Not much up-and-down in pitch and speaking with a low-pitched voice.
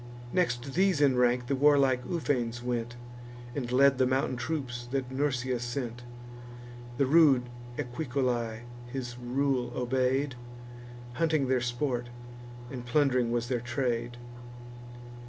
Yes: narrow, 2.2 semitones; low, 125 Hz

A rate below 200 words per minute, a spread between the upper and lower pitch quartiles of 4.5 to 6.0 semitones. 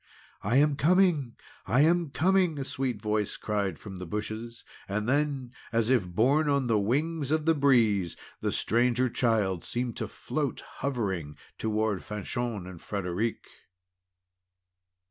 Yes: average, 140 wpm; average, 5.1 semitones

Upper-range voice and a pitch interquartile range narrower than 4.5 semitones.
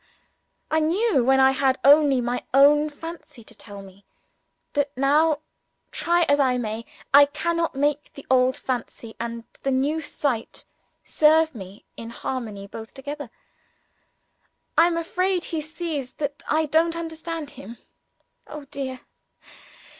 Yes: very high, 285 Hz; average, 4.0 semitones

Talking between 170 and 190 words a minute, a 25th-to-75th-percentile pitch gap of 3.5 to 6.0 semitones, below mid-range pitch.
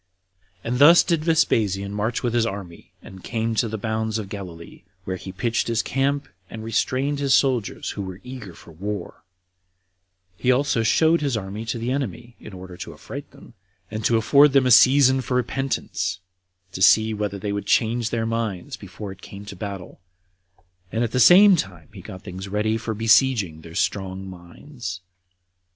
Yes: average, 185 wpm; average, 4.5 semitones; low, 110 Hz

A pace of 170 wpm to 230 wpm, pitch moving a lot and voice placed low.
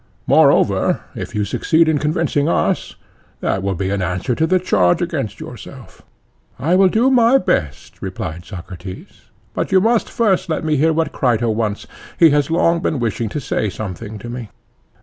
Yes: average, 175 wpm; wide, 8.8 semitones; low, 130 Hz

